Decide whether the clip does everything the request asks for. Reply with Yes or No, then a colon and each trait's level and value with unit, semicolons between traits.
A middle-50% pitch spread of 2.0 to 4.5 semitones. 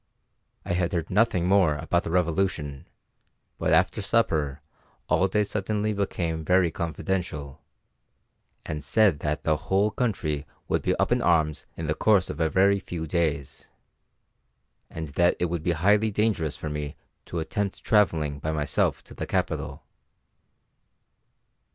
Yes: average, 4.0 semitones